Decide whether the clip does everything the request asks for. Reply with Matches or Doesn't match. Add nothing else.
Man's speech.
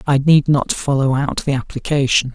Matches